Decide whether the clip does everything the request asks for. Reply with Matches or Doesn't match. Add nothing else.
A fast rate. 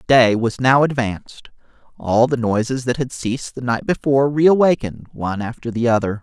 Doesn't match